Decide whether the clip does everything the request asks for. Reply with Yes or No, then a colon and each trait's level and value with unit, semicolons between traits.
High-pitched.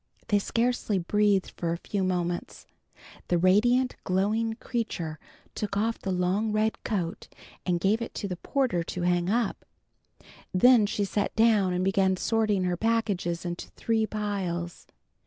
Yes: high, 200 Hz